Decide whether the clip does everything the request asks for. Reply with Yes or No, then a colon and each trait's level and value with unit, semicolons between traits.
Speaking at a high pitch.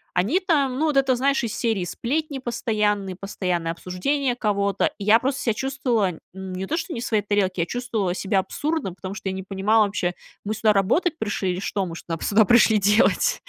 Yes: high, 210 Hz